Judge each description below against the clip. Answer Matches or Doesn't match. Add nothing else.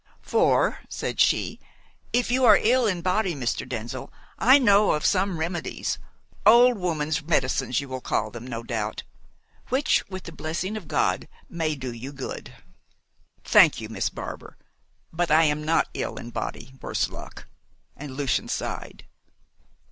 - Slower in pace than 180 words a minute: Matches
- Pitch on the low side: Doesn't match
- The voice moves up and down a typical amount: Doesn't match